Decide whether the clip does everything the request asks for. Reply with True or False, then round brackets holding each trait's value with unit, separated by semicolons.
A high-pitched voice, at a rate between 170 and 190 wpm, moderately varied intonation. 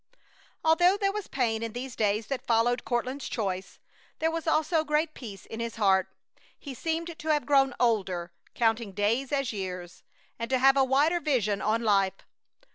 False (245 Hz; 175 wpm; 6.0 semitones)